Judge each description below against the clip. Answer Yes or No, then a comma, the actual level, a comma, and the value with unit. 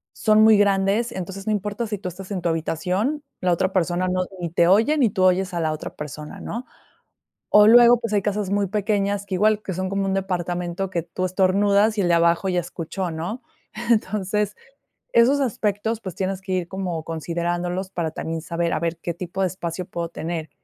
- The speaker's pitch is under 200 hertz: Yes, high, 190 Hz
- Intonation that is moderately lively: Yes, average, 3.1 semitones